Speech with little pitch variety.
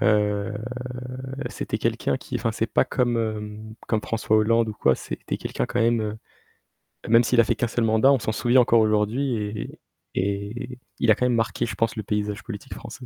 Yes: narrow, 2.1 semitones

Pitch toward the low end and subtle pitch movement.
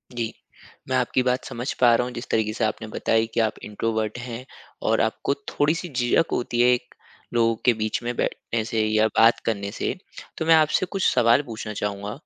Yes: low, 115 Hz; narrow, 2.2 semitones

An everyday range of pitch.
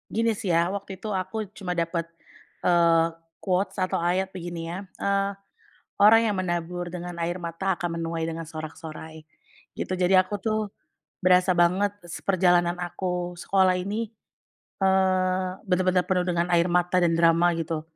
No: narrow, 1.8 semitones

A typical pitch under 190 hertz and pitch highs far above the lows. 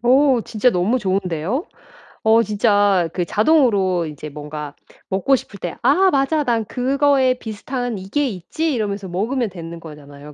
No: high, 210 Hz; wide, 6.4 semitones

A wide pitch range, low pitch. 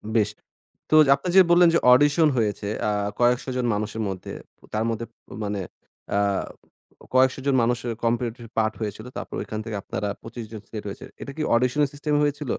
No: average, 4.1 semitones; low, 120 Hz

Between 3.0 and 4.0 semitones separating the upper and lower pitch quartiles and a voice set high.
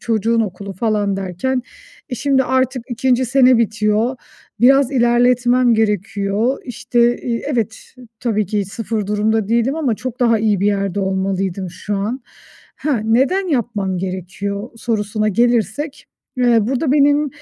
Yes: average, 3.7 semitones; high, 230 Hz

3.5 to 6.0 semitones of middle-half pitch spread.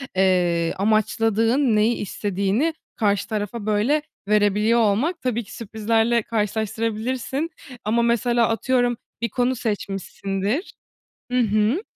No: narrow, 2.5 semitones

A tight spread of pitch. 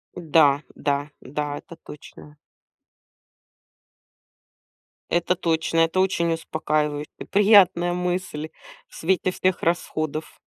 No: average, 3.0 semitones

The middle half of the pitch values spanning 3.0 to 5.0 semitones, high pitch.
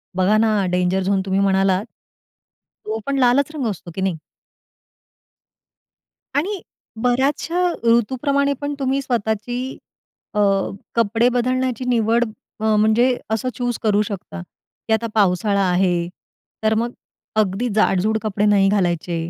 Yes: average, 4.1 semitones; high, 220 Hz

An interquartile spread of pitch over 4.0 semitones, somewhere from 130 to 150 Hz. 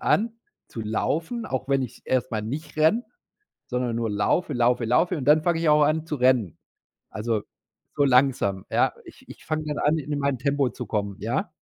Yes: average, 4.6 semitones; low, 135 Hz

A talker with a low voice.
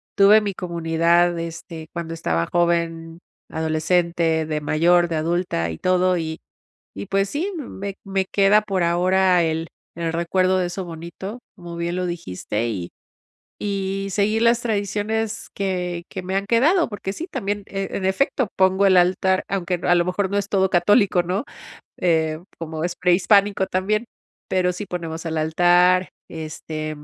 No: medium, 180 Hz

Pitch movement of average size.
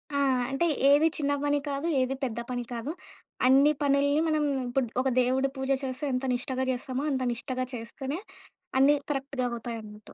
No: narrow, 2.2 semitones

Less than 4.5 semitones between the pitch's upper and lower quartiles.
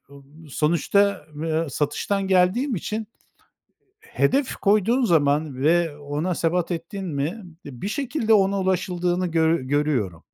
No: average, 4.9 semitones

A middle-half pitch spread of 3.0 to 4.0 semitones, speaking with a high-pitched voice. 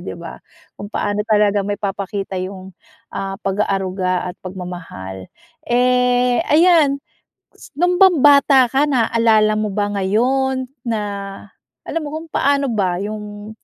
No: average, 5.3 semitones; high, 215 Hz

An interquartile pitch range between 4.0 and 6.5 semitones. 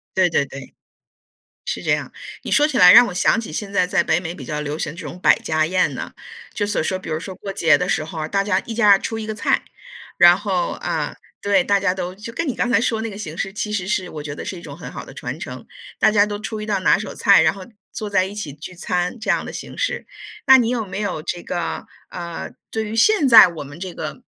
No: average, 3.6 semitones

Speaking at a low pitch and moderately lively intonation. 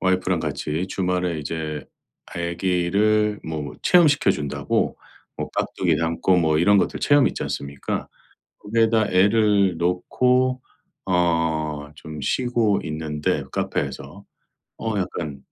Yes: very low, 90 Hz; average, 4.8 semitones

